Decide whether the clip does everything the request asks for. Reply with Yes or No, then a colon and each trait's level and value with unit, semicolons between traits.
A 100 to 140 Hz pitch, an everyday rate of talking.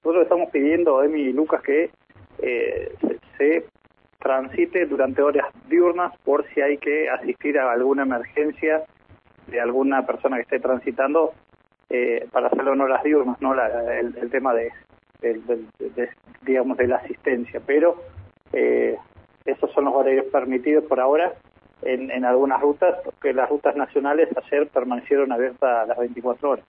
Yes: low, 135 Hz; average, 165 wpm